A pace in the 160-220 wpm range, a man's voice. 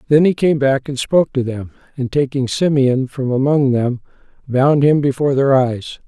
Yes: average, 190 wpm; male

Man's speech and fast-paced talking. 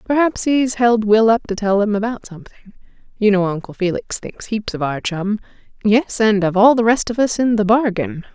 No: female; fast, 215 wpm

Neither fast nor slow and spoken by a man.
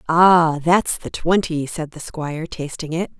No: average, 170 wpm; female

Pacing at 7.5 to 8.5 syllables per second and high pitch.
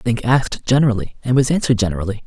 No: 7.8 syllables/s; low, 115 Hz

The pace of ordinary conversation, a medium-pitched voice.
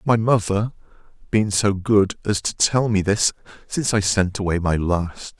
No: average, 180 wpm; low, 100 Hz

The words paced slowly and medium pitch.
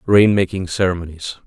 No: slow, 125 wpm; very low, 90 Hz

